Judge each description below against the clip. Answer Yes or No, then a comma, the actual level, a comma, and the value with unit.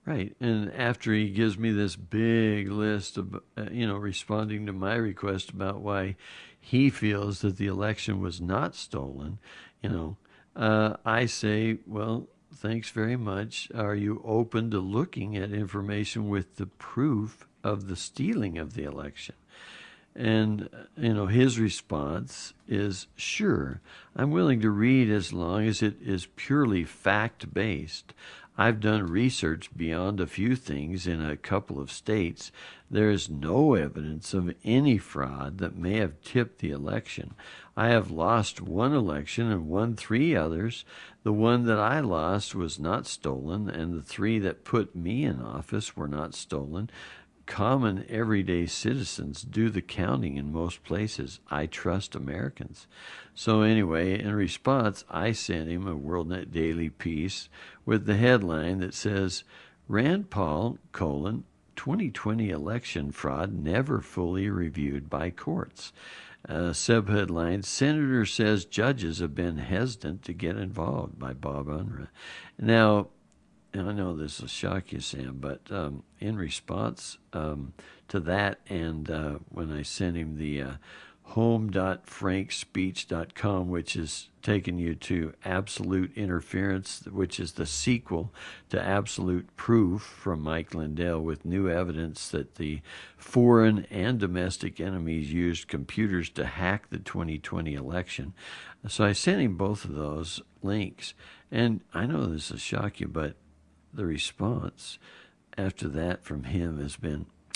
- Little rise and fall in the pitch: No, average, 4.7 semitones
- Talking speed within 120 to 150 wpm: Yes, average, 145 wpm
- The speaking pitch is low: Yes, very low, 95 Hz